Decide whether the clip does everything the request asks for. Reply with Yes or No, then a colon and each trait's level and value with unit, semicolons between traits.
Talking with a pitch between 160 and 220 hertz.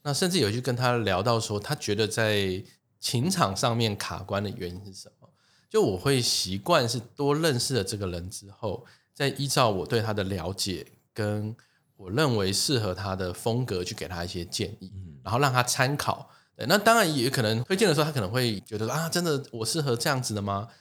No: low, 115 Hz